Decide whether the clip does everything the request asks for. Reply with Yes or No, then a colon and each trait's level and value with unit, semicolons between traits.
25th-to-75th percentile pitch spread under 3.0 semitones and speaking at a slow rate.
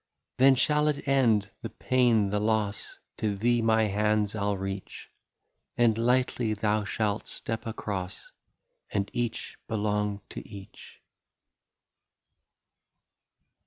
Yes: narrow, 2.5 semitones; slow, 120 wpm